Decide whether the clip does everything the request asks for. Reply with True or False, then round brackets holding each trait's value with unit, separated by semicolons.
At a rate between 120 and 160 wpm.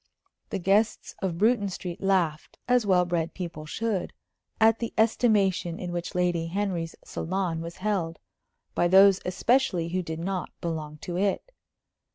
True (150 wpm)